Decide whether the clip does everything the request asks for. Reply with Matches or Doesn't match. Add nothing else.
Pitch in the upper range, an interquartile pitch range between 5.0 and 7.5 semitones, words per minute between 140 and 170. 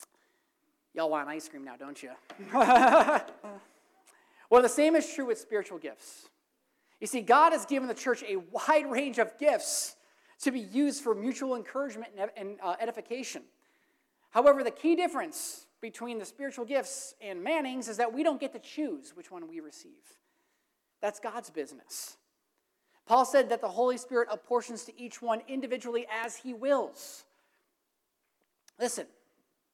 Matches